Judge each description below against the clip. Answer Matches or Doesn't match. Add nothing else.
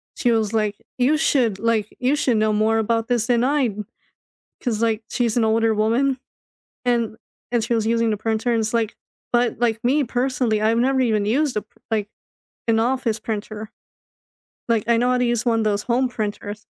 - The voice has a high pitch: Matches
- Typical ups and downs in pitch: Doesn't match